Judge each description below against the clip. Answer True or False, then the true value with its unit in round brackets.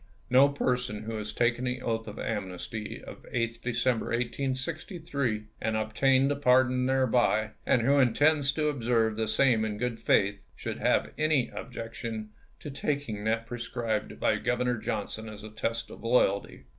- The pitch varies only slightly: False (3.0 semitones)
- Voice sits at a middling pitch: False (120 Hz)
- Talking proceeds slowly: False (155 wpm)